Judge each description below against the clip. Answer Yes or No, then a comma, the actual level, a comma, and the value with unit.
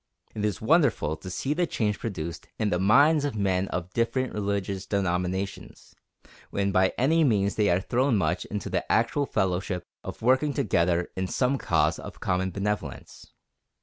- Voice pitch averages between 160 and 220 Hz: No, low, 100 Hz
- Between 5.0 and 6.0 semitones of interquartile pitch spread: Yes, wide, 5.4 semitones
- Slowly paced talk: No, average, 165 wpm